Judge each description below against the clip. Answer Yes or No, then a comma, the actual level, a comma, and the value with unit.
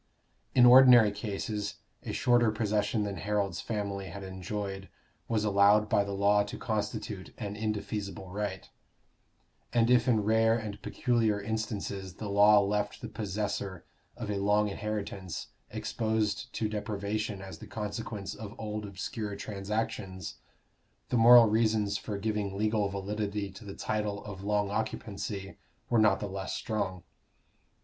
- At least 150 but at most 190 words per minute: No, average, 140 wpm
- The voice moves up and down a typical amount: No, narrow, 1.5 semitones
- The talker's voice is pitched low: Yes, low, 105 Hz